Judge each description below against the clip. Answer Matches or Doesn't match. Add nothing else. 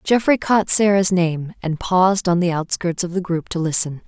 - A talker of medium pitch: Matches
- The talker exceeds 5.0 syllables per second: Doesn't match